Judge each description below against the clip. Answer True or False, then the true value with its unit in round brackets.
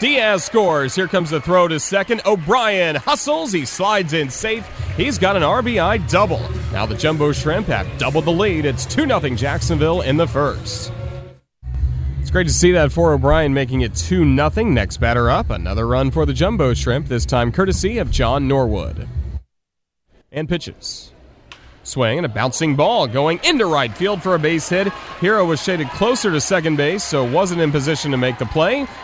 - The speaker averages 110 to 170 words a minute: False (185 wpm)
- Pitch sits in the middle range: True (150 Hz)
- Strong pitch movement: True (6.7 semitones)